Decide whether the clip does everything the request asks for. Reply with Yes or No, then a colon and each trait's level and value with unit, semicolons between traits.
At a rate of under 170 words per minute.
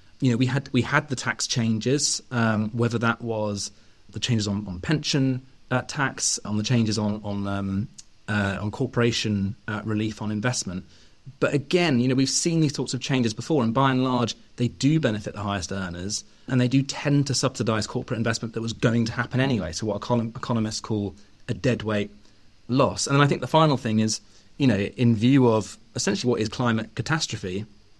No: average, 200 wpm